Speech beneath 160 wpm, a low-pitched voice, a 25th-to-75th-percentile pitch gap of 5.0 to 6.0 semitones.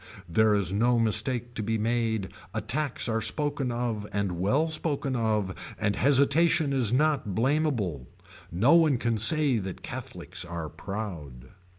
Yes: average, 145 wpm; low, 115 Hz; wide, 5.4 semitones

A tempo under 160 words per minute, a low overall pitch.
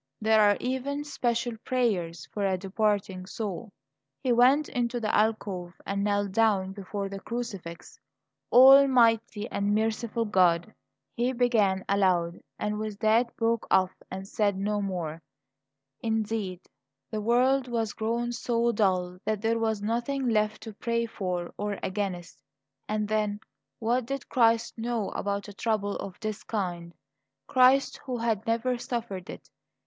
No: average, 145 wpm; high, 215 Hz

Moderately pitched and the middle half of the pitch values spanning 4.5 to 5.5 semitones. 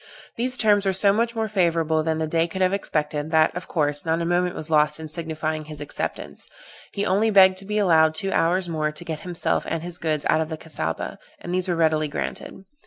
No: medium, 165 Hz; average, 3.2 semitones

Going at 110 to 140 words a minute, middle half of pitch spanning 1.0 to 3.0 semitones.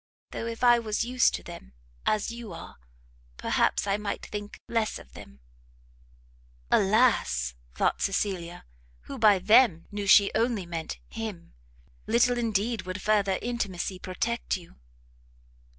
No: slow, 135 wpm; average, 3.9 semitones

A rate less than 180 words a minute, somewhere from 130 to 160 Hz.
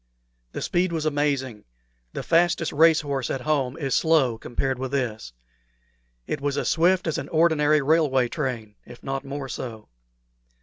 Yes: average, 160 wpm; medium, 140 Hz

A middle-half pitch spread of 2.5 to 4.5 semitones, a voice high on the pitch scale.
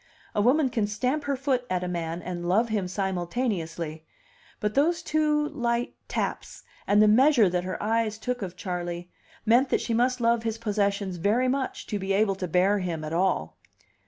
No: wide, 5.4 semitones; high, 210 Hz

